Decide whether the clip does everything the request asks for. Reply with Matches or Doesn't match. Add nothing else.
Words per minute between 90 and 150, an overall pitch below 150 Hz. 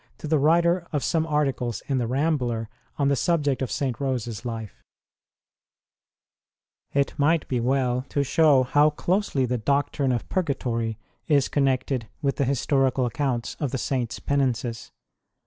Doesn't match